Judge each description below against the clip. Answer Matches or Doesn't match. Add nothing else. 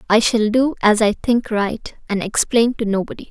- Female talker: Matches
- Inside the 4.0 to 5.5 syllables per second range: Matches